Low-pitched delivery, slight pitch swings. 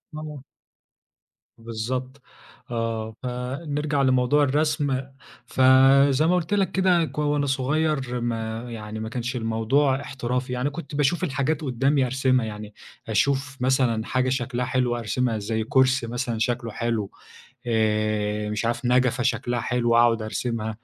No: low, 125 Hz; average, 3.2 semitones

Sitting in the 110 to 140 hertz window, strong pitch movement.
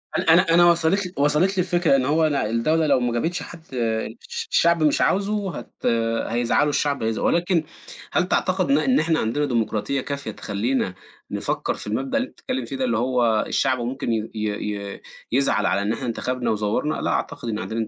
Yes: low, 135 Hz; wide, 6.6 semitones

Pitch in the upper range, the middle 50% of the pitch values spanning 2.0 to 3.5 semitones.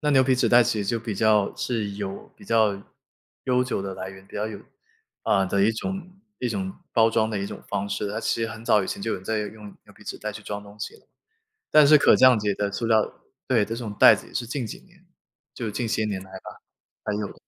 No: low, 110 Hz; average, 2.8 semitones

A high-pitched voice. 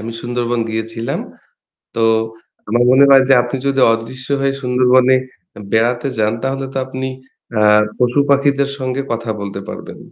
No: low, 125 Hz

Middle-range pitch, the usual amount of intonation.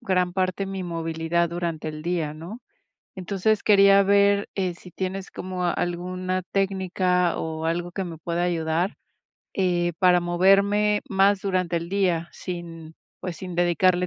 No: medium, 180 Hz; narrow, 2.1 semitones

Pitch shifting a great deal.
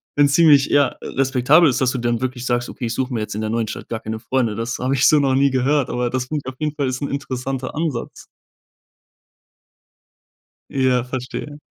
No: narrow, 2.4 semitones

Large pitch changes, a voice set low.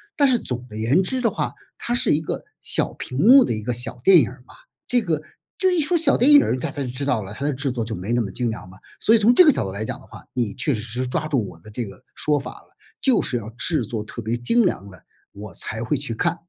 Yes: wide, 8.7 semitones; low, 125 Hz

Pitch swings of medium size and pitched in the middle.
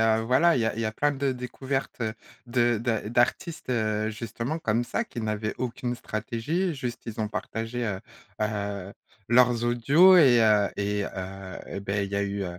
No: average, 3.1 semitones; low, 115 Hz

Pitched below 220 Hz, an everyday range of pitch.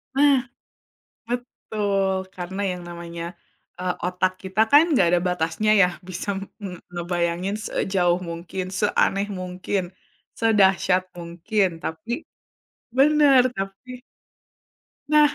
Yes: high, 190 Hz; average, 3.3 semitones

